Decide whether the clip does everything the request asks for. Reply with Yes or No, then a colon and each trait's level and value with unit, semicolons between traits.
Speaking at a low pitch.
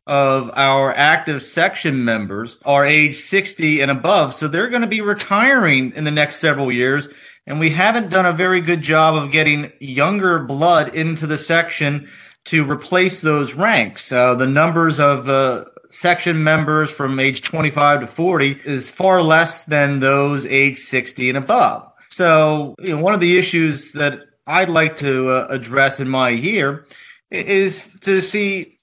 No: medium, 150 Hz